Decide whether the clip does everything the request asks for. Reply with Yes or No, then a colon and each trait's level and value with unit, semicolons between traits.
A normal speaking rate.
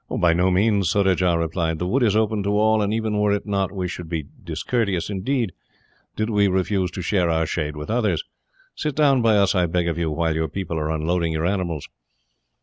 No: fast, 215 wpm